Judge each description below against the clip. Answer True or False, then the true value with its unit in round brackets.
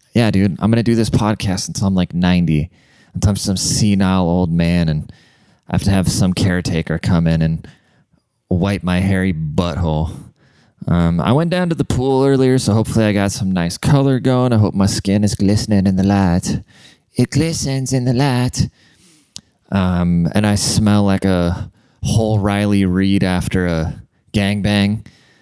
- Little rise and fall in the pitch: False (3.9 semitones)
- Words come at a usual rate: True (175 wpm)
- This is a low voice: True (100 Hz)